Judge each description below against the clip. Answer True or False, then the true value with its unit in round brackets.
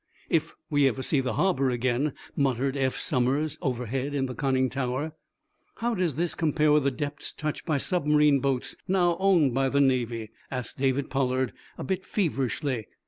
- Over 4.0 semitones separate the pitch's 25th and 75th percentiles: False (2.8 semitones)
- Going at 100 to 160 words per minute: False (170 wpm)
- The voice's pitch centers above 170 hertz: False (135 Hz)